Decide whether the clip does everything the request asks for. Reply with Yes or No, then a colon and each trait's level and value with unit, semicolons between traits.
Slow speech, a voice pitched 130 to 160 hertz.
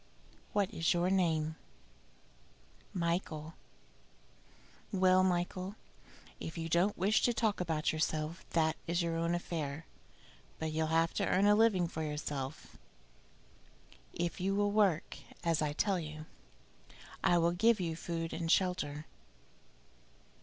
No: slow, 130 wpm; medium, 170 Hz